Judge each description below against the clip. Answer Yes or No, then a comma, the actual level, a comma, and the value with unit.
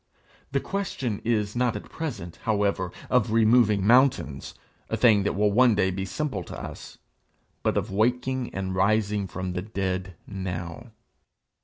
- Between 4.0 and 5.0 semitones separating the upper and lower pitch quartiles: Yes, average, 4.3 semitones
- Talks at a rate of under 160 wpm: Yes, average, 150 wpm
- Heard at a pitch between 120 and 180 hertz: No, low, 105 Hz